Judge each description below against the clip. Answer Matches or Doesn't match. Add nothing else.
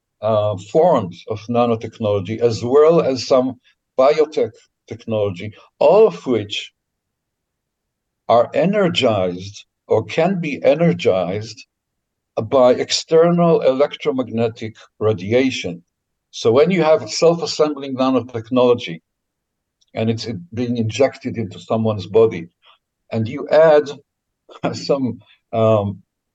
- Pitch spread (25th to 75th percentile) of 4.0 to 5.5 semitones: Matches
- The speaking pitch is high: Doesn't match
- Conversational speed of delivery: Doesn't match